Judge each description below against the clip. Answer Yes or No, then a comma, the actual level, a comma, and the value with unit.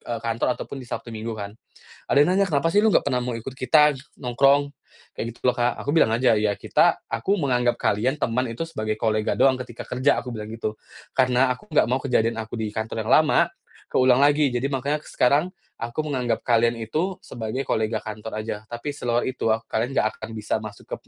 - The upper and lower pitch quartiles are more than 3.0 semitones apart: Yes, average, 3.6 semitones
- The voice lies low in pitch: Yes, low, 120 Hz